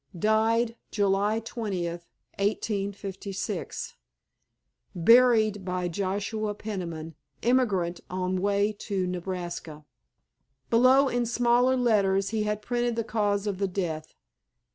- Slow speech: Yes, slow, 100 wpm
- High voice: Yes, high, 205 Hz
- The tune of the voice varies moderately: Yes, average, 3.5 semitones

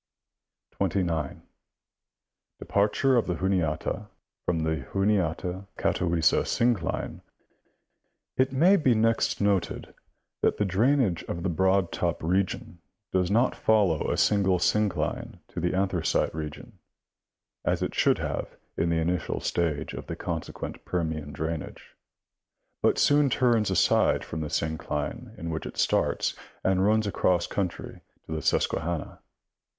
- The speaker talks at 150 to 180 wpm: No, slow, 135 wpm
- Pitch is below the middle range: Yes, very low, 90 Hz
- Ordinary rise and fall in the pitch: Yes, average, 4.3 semitones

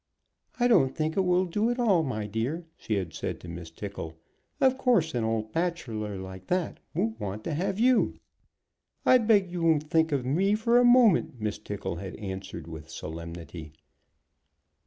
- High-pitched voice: No, low, 135 Hz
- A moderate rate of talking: Yes, average, 180 wpm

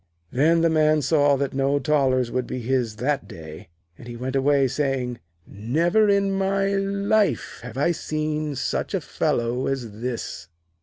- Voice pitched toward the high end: No, medium, 140 Hz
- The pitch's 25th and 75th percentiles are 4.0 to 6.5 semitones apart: Yes, average, 4.3 semitones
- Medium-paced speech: Yes, average, 160 wpm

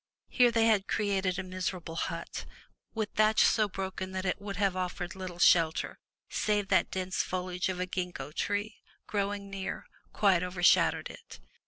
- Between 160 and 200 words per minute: Yes, average, 165 wpm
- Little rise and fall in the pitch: Yes, narrow, 1.9 semitones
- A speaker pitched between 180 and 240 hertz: Yes, high, 190 Hz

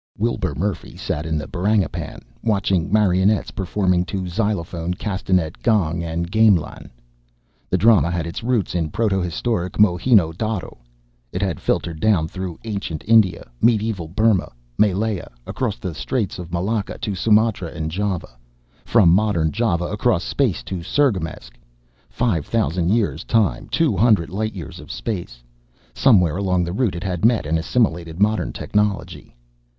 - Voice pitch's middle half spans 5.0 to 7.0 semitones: No, average, 4.2 semitones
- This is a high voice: No, very low, 95 Hz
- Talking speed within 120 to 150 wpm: Yes, average, 145 wpm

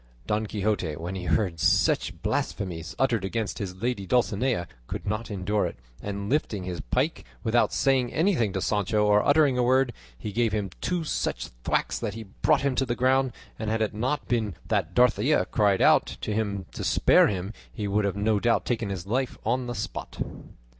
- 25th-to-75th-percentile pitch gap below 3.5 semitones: No, average, 3.8 semitones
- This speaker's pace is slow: No, average, 195 wpm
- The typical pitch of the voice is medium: No, low, 110 Hz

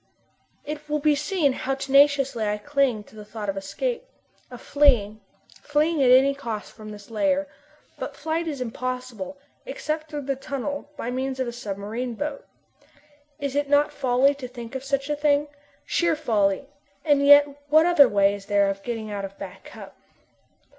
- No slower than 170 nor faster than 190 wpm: Yes, average, 175 wpm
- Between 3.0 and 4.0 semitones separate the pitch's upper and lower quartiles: No, average, 4.6 semitones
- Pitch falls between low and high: No, very high, 270 Hz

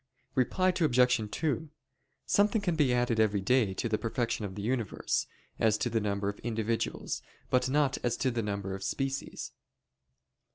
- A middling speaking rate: Yes, average, 165 wpm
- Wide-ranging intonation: No, average, 3.9 semitones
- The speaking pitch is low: Yes, low, 120 Hz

